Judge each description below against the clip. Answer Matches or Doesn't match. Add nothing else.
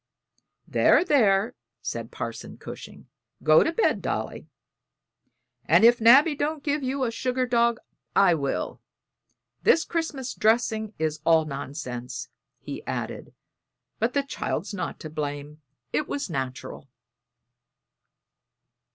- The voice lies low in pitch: Doesn't match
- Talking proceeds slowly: Matches